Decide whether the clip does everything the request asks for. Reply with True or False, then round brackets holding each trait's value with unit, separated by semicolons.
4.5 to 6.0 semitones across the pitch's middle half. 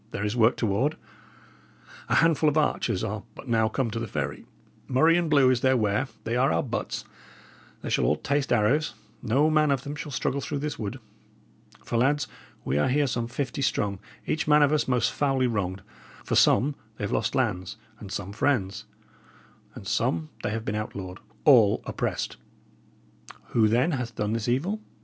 True (5.2 semitones)